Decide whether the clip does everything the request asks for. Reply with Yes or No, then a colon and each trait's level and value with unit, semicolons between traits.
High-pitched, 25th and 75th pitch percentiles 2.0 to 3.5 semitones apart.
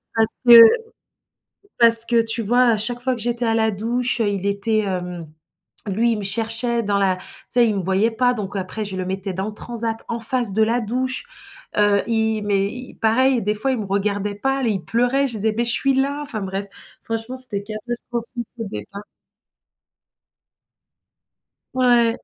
Yes: high, 225 Hz; average, 2.9 semitones